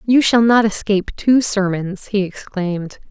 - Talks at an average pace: Yes, average, 155 wpm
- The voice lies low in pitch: No, high, 205 Hz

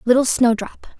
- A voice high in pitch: Yes, high, 240 Hz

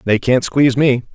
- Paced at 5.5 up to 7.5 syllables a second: No, 5.2 syllables/s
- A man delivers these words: Yes, male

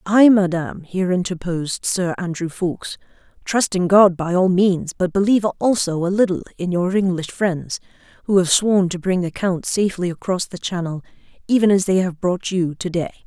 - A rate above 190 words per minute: No, average, 185 wpm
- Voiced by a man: No, female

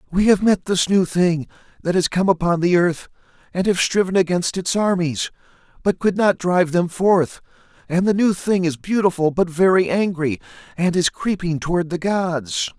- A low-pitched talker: No, medium, 175 Hz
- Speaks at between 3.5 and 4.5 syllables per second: No, 4.9 syllables/s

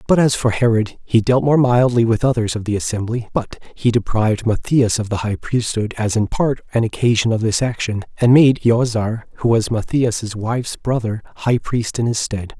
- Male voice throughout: Yes, male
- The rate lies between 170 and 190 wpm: No, average, 200 wpm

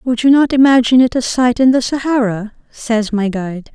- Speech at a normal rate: No, fast, 210 wpm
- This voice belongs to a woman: Yes, female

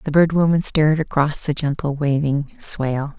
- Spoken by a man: No, female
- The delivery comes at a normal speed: Yes, average, 170 wpm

